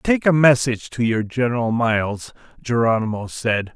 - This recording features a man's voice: Yes, male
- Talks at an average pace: Yes, average, 145 wpm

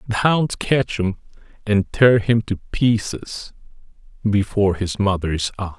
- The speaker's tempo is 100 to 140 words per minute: Yes, slow, 135 wpm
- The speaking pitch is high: No, low, 105 Hz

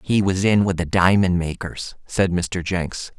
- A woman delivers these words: No, male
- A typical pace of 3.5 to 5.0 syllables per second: Yes, 4.0 syllables/s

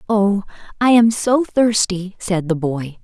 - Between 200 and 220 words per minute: No, average, 160 wpm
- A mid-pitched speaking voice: No, high, 205 Hz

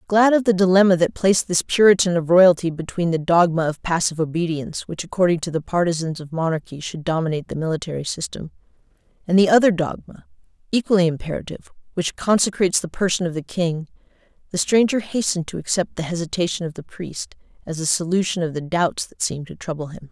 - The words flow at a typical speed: Yes, average, 185 wpm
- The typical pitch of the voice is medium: Yes, medium, 175 Hz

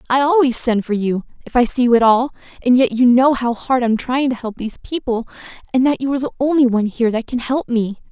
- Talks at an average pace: No, fast, 250 wpm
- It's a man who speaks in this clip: No, female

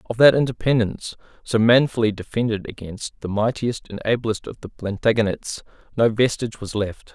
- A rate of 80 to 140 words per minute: No, average, 150 wpm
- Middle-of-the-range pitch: No, low, 110 Hz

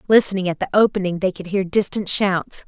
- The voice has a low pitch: No, high, 190 Hz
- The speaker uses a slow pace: No, average, 200 wpm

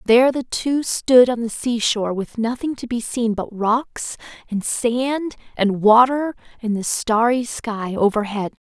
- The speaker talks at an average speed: Yes, average, 165 wpm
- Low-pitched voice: No, high, 235 Hz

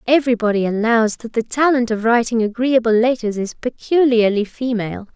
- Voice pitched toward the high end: Yes, high, 235 Hz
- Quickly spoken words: No, average, 140 wpm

